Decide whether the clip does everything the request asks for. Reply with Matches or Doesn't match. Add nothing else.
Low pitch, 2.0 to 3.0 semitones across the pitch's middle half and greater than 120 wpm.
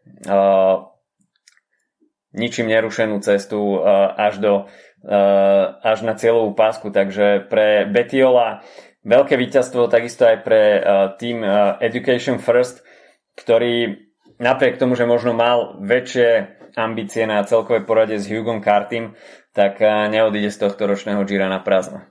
Matches